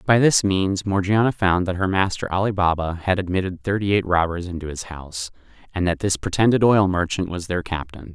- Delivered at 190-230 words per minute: Yes, average, 200 wpm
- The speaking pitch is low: Yes, very low, 95 Hz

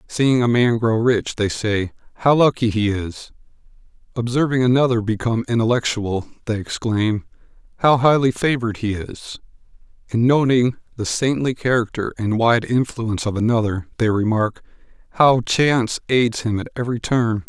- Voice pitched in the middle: No, low, 115 Hz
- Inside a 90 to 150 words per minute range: Yes, average, 140 wpm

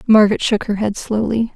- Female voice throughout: Yes, female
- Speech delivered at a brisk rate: No, average, 195 wpm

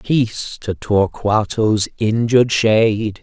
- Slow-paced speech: Yes, slow, 95 wpm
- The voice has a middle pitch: No, low, 110 Hz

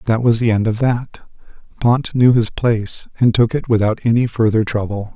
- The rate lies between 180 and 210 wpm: Yes, average, 200 wpm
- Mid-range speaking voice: No, low, 115 Hz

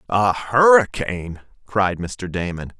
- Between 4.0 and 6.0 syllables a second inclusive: No, 3.8 syllables/s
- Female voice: No, male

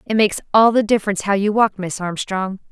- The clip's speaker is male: No, female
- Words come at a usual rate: No, fast, 220 wpm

